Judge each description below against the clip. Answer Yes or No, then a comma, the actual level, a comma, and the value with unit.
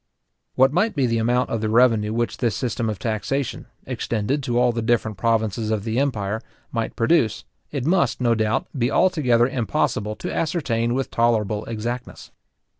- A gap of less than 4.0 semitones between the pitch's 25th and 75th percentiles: Yes, narrow, 2.5 semitones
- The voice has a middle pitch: No, low, 115 Hz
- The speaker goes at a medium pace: Yes, average, 170 wpm